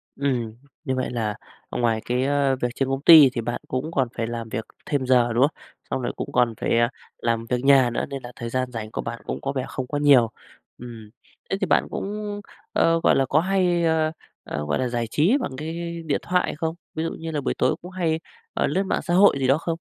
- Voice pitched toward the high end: No, low, 135 Hz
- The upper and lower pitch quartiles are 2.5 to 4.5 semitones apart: No, average, 5.2 semitones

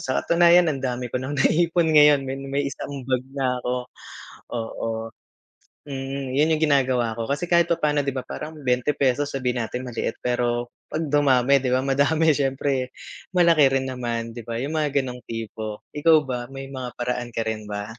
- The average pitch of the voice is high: No, low, 135 Hz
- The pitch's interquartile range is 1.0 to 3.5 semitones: Yes, average, 2.9 semitones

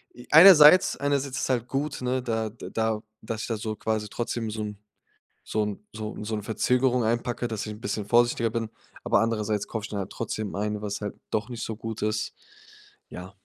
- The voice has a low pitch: Yes, low, 110 Hz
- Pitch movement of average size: No, narrow, 2.3 semitones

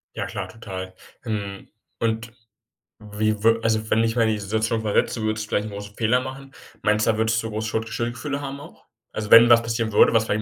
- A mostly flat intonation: Yes, narrow, 1.4 semitones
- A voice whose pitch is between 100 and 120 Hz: Yes, low, 110 Hz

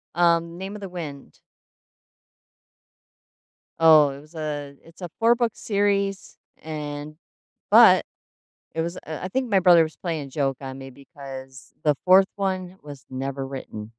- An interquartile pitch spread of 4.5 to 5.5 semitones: Yes, average, 4.8 semitones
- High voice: No, medium, 160 Hz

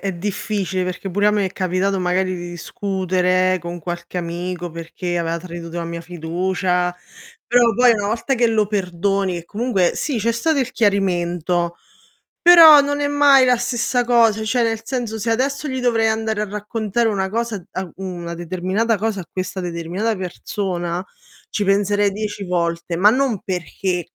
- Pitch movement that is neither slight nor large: Yes, average, 4.1 semitones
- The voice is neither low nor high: No, high, 195 Hz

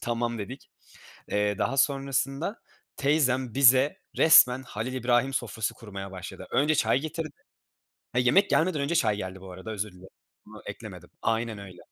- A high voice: No, low, 125 Hz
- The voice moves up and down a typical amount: Yes, average, 4.8 semitones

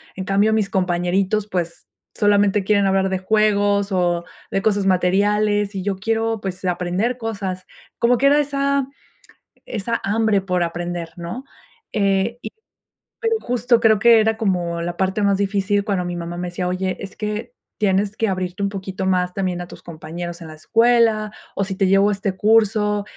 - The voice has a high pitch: Yes, high, 195 Hz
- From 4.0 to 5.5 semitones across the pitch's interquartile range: No, average, 2.7 semitones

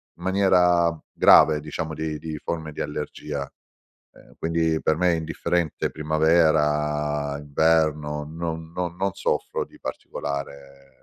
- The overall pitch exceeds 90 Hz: No, very low, 80 Hz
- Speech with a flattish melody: Yes, narrow, 2.0 semitones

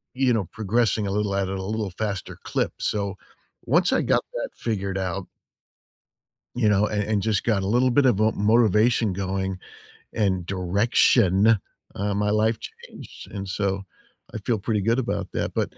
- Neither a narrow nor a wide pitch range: No, narrow, 2.3 semitones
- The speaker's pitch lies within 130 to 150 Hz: No, low, 105 Hz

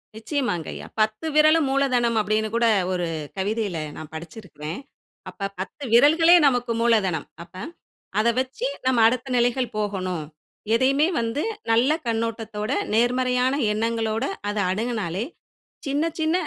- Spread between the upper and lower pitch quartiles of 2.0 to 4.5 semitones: Yes, average, 3.8 semitones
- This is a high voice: Yes, high, 230 Hz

